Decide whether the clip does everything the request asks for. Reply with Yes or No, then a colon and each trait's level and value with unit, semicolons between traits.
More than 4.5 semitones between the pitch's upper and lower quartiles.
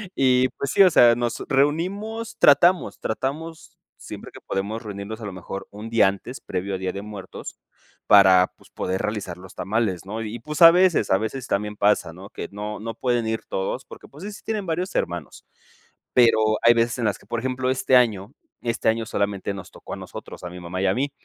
Yes: average, 5.1 semitones